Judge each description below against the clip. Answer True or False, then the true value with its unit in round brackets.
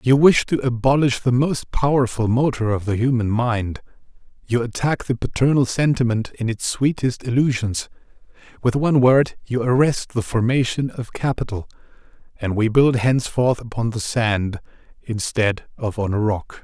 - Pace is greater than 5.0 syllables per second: False (4.8 syllables/s)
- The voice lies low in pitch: True (120 Hz)